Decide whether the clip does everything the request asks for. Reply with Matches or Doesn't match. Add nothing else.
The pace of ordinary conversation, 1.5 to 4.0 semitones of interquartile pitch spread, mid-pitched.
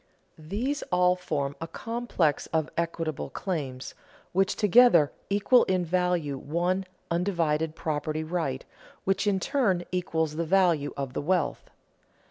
Doesn't match